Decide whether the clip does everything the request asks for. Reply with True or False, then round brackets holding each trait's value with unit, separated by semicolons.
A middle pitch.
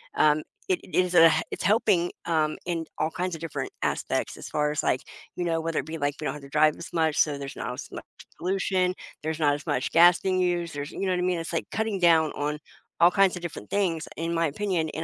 True (165 Hz)